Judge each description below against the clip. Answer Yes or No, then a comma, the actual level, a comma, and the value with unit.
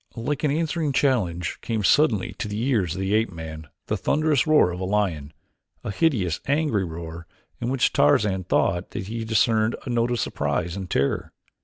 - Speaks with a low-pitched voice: Yes, low, 105 Hz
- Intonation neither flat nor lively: No, wide, 6.5 semitones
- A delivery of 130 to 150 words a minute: No, average, 185 wpm